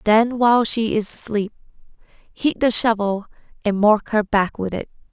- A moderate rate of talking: Yes, average, 165 wpm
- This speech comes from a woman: Yes, female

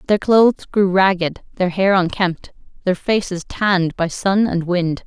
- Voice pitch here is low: No, medium, 185 Hz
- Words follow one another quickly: No, average, 165 wpm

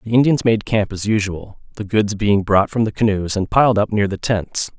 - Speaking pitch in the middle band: No, low, 105 Hz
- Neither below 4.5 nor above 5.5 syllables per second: Yes, 5.1 syllables/s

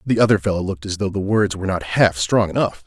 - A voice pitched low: Yes, very low, 95 Hz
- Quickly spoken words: Yes, fast, 275 wpm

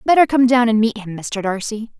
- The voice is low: No, high, 225 Hz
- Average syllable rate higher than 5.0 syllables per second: Yes, 5.5 syllables/s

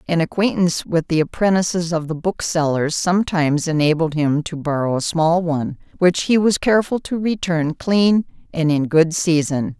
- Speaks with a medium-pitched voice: Yes, medium, 165 Hz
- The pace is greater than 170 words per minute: No, average, 165 wpm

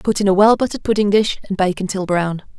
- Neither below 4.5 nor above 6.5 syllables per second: Yes, 6.4 syllables/s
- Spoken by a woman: Yes, female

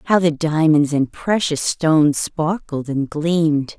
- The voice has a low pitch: No, medium, 155 Hz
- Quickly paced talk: No, average, 145 wpm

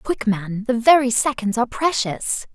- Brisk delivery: No, average, 165 wpm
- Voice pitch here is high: Yes, high, 240 Hz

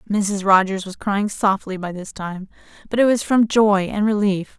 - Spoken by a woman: Yes, female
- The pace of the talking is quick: No, average, 195 wpm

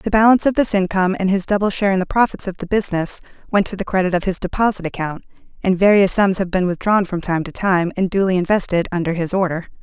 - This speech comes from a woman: Yes, female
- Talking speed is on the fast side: Yes, fast, 240 wpm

